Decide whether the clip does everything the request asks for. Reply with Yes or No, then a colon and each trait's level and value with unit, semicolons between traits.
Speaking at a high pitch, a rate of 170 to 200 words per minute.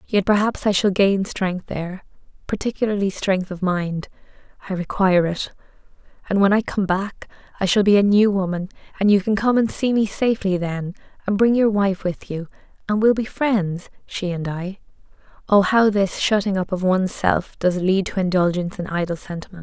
Yes: high, 195 Hz; average, 180 wpm